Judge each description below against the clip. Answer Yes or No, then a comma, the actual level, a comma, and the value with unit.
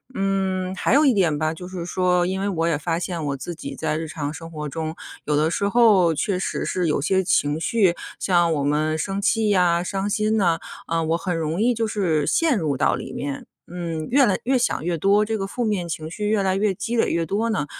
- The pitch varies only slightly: No, average, 4.0 semitones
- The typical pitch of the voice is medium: Yes, medium, 180 Hz